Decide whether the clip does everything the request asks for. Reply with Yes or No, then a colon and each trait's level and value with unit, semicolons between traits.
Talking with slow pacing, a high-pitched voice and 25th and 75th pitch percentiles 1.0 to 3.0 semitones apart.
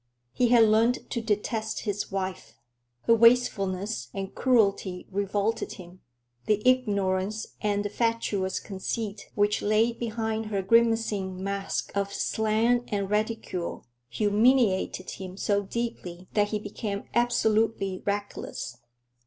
Yes: slow, 120 wpm; high, 210 Hz; narrow, 2.6 semitones